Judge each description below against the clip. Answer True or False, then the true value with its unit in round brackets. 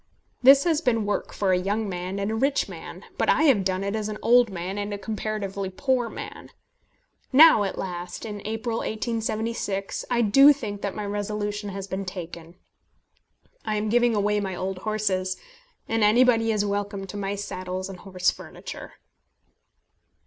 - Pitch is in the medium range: False (205 Hz)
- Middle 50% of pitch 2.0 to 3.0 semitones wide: True (2.7 semitones)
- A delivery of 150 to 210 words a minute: True (170 wpm)